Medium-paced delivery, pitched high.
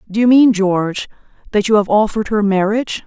Yes: average, 195 wpm; high, 210 Hz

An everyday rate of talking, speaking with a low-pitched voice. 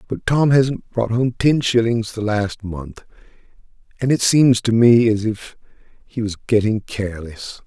Yes: average, 165 wpm; low, 115 Hz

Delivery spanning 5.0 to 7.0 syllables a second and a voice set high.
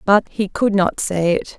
No: 4.2 syllables/s; high, 195 Hz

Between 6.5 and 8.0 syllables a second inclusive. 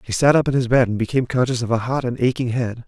Yes: 7.0 syllables/s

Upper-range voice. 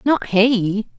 Yes: high, 210 Hz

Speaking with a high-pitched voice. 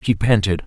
No: low, 105 Hz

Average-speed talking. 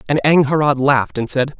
Yes: average, 190 wpm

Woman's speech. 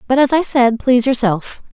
Yes: female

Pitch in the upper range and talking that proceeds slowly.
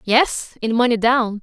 Yes: high, 235 Hz; slow, 125 wpm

